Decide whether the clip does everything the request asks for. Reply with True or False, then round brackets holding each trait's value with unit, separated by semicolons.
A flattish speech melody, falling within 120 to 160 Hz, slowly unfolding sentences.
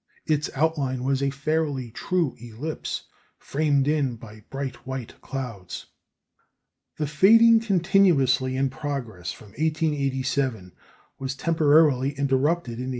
False (3.3 semitones; 140 Hz; 115 wpm)